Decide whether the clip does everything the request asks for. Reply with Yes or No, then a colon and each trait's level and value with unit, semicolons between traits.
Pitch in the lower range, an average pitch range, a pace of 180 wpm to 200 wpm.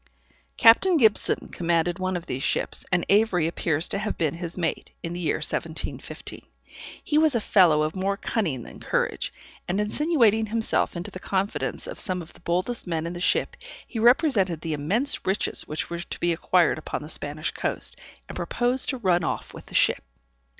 No: medium, 185 Hz; average, 4.9 semitones; average, 190 wpm